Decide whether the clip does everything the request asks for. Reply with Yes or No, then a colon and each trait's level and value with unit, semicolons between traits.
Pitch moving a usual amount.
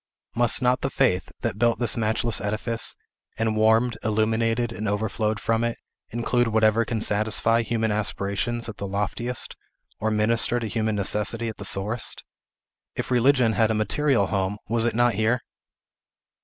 No: narrow, 1.7 semitones